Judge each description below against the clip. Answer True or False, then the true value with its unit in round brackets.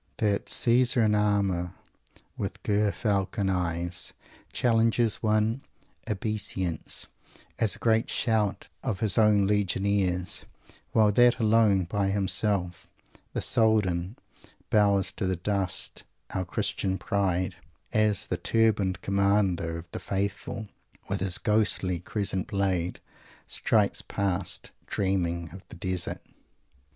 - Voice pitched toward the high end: False (100 Hz)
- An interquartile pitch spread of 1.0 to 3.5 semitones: True (2.5 semitones)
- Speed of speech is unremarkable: False (115 wpm)